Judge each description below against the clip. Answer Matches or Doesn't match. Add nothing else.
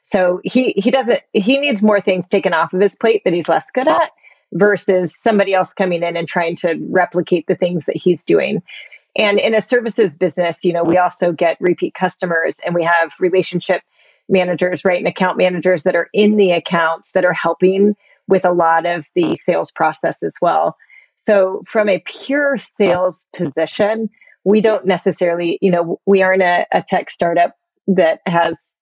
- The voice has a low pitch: Doesn't match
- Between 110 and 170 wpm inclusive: Doesn't match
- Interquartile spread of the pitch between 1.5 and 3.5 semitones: Matches